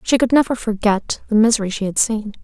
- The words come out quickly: Yes, fast, 220 wpm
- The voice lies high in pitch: Yes, high, 220 Hz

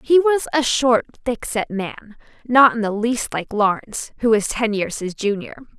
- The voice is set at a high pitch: Yes, high, 230 Hz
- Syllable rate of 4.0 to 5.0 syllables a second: Yes, 4.6 syllables/s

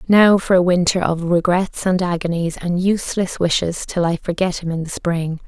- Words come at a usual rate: Yes, average, 195 wpm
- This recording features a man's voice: No, female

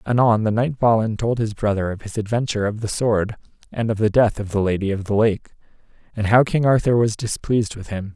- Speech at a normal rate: No, fast, 230 wpm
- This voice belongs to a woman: No, male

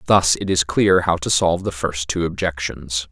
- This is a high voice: No, very low, 85 Hz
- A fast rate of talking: Yes, fast, 210 wpm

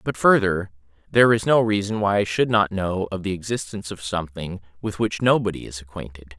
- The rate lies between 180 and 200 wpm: Yes, average, 195 wpm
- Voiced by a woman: No, male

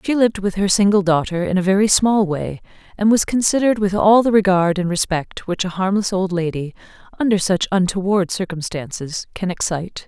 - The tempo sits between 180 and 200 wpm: Yes, average, 185 wpm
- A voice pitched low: No, high, 190 Hz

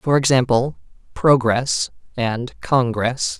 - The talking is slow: Yes, slow, 90 wpm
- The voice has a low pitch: Yes, low, 125 Hz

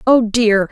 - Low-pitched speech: No, high, 225 Hz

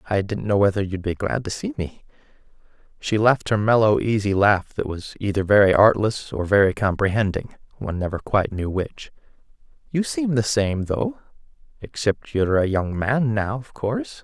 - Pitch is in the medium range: No, low, 105 Hz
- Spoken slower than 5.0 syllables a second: No, 5.3 syllables/s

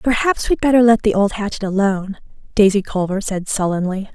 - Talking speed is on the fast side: No, average, 175 wpm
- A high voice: Yes, high, 205 Hz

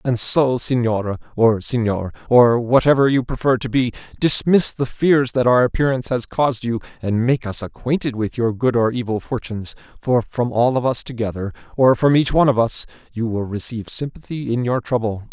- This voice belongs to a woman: No, male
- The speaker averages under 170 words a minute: No, average, 190 wpm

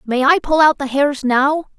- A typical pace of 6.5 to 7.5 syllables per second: No, 4.3 syllables/s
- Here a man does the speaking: No, female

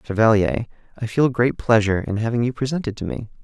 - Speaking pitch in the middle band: No, low, 115 Hz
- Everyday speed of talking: Yes, average, 190 wpm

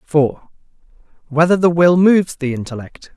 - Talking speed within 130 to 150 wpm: Yes, slow, 135 wpm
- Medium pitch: Yes, medium, 160 Hz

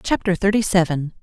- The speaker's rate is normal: Yes, average, 145 wpm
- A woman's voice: Yes, female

